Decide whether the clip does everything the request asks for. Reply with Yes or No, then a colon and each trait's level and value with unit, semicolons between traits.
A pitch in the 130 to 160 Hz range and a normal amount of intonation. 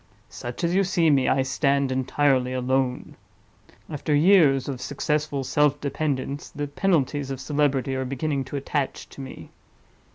No: medium, 140 Hz; narrow, 2.1 semitones